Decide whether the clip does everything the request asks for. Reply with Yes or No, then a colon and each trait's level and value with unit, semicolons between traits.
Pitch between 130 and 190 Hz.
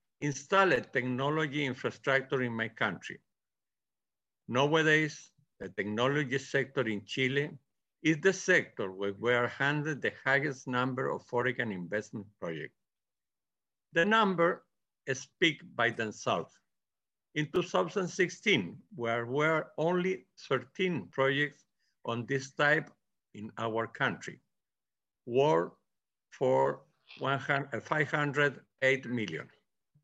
Yes: medium, 140 Hz